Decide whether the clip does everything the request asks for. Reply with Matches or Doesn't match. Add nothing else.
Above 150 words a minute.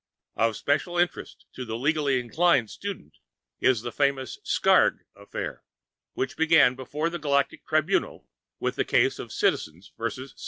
Doesn't match